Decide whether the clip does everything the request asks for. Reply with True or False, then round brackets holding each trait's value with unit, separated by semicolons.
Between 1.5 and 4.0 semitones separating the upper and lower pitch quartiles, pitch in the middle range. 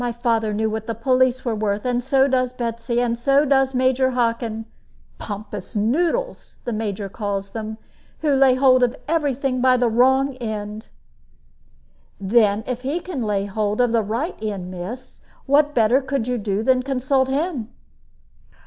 False (3.3 semitones; 245 Hz)